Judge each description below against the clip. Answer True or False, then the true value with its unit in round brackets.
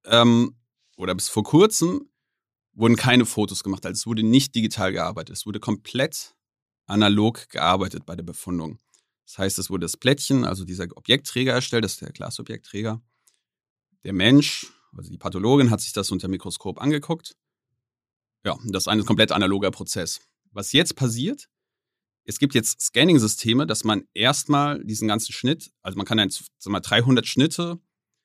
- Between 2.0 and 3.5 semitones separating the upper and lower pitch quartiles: False (4.7 semitones)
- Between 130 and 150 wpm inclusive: False (160 wpm)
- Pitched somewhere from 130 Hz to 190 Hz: False (110 Hz)